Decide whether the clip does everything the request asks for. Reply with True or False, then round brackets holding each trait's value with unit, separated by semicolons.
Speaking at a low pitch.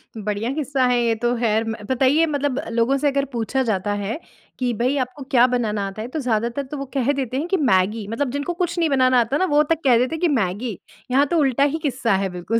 False (255 Hz)